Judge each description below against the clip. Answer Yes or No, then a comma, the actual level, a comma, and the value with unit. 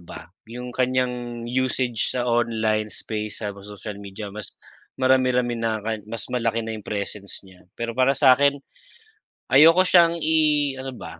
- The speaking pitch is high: No, low, 120 Hz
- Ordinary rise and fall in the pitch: Yes, average, 3.4 semitones